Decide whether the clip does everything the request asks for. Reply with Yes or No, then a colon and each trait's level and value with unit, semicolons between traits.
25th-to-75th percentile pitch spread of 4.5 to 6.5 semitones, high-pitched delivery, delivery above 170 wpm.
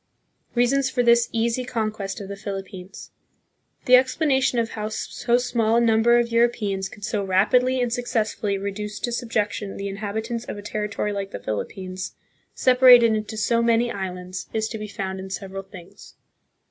No: average, 3.3 semitones; high, 215 Hz; average, 185 wpm